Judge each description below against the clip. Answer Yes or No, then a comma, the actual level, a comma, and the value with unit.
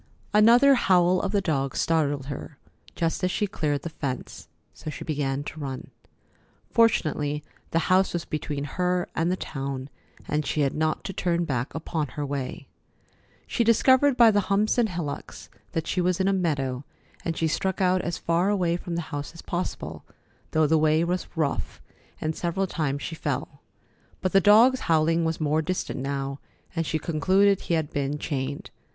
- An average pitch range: Yes, average, 4.0 semitones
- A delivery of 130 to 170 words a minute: No, average, 180 wpm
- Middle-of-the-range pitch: Yes, medium, 165 Hz